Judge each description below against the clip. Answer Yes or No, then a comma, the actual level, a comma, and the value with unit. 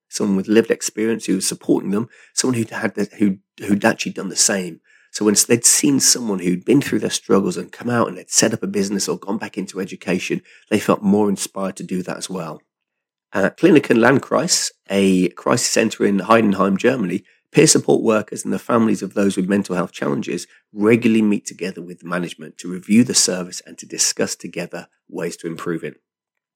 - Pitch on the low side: Yes, low, 100 Hz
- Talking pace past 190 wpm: Yes, fast, 205 wpm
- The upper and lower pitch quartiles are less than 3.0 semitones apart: Yes, narrow, 2.6 semitones